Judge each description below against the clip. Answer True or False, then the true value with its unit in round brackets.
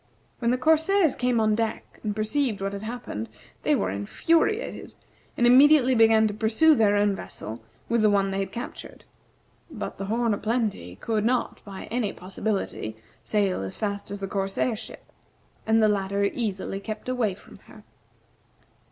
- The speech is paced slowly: False (170 wpm)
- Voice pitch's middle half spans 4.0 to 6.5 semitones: False (3.5 semitones)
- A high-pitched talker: True (215 Hz)